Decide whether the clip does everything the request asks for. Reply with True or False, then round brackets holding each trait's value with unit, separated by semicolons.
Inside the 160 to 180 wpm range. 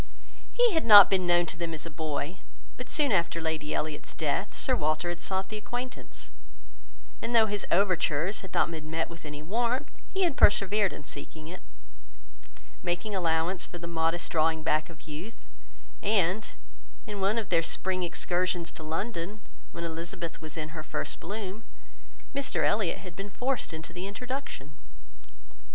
True (170 wpm)